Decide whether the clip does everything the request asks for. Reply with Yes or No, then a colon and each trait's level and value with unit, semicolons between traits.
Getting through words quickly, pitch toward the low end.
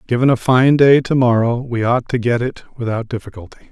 Yes: fast, 210 wpm; low, 120 Hz